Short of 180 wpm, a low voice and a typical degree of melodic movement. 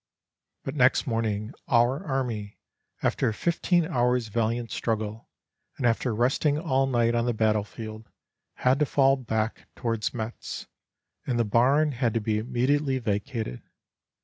Yes: average, 140 wpm; low, 120 Hz; average, 3.2 semitones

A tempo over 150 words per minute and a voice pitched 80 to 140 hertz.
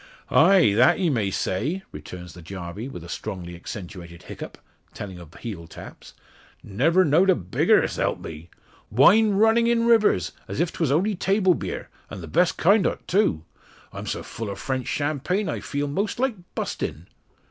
Yes: average, 170 wpm; low, 135 Hz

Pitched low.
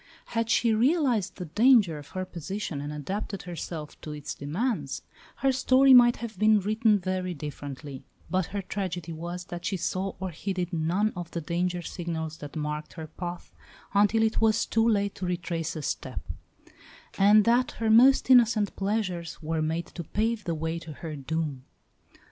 No: medium, 180 Hz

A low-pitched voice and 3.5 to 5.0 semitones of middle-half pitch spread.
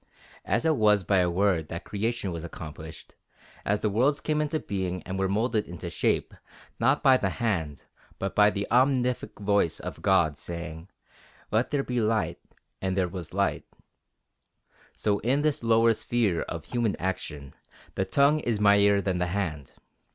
Yes: low, 100 Hz; average, 4.7 semitones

